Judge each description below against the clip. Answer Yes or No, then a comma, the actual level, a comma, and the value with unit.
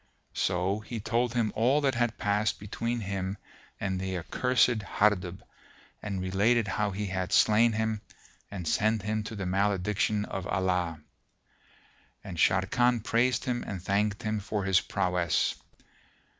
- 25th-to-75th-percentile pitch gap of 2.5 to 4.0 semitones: Yes, average, 2.9 semitones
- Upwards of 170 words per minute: No, average, 145 wpm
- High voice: No, low, 105 Hz